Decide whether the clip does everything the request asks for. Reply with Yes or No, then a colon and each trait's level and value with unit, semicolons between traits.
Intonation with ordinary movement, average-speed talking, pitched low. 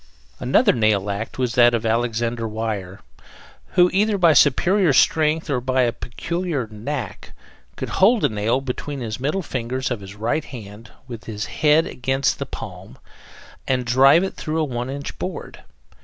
Yes: average, 5.0 semitones; average, 165 wpm; low, 125 Hz